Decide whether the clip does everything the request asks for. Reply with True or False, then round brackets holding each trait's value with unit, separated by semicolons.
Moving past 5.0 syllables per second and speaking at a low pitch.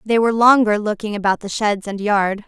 False (5.5 syllables/s; 210 Hz)